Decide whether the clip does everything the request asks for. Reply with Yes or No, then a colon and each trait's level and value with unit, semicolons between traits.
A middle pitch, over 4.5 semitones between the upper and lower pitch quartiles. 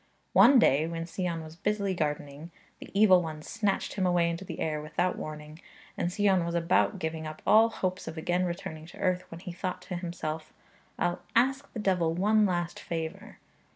No: medium, 175 Hz; average, 3.0 semitones